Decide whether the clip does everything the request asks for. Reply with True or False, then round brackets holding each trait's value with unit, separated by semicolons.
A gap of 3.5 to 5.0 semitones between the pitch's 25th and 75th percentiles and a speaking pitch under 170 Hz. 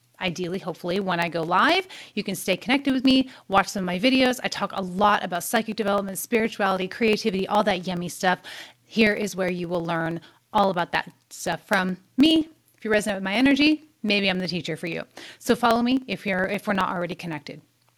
False (3.9 semitones; 195 Hz)